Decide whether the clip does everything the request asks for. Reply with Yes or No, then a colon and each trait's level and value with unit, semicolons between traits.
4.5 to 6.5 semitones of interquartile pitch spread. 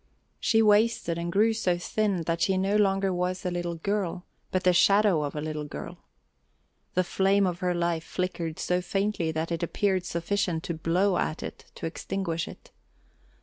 No: average, 2.8 semitones